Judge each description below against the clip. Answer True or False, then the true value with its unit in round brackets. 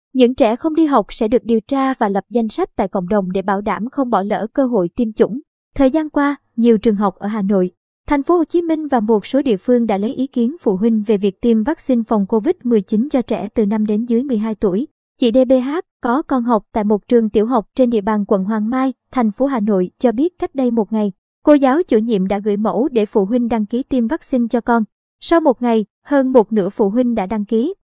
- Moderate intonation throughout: True (3.5 semitones)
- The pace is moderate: False (255 wpm)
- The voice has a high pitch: True (235 Hz)